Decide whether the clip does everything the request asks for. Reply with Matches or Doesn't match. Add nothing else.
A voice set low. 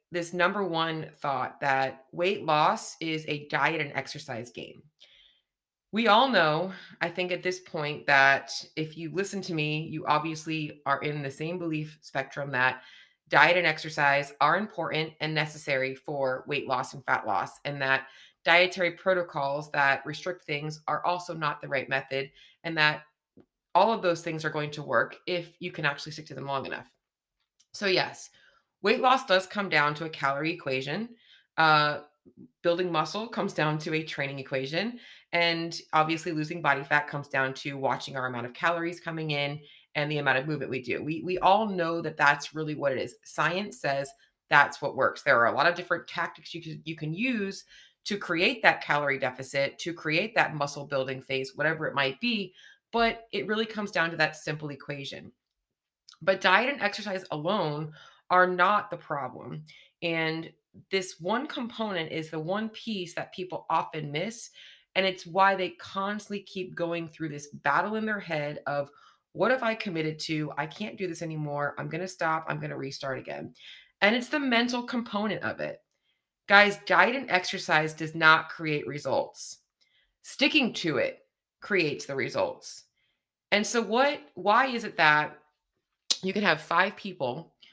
Doesn't match